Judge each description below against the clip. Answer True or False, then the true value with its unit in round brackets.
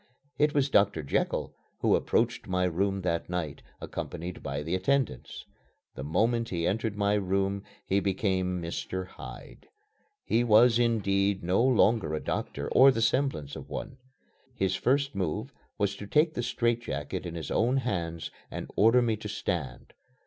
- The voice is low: True (100 Hz)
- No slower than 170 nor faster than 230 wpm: False (155 wpm)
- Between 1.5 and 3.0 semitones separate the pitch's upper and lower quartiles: False (4.6 semitones)